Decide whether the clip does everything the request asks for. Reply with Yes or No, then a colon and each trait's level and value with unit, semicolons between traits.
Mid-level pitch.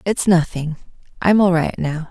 Yes: medium, 175 Hz